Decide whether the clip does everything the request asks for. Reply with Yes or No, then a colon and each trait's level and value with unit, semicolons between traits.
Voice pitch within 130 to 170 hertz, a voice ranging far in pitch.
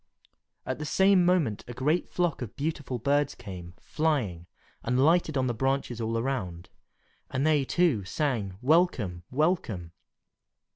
Yes: low, 135 Hz; wide, 6.1 semitones